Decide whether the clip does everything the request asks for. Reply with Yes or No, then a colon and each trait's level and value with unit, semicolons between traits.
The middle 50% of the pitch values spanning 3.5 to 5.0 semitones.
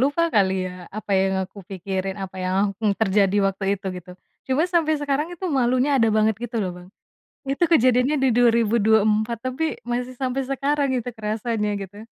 Yes: average, 4.5 semitones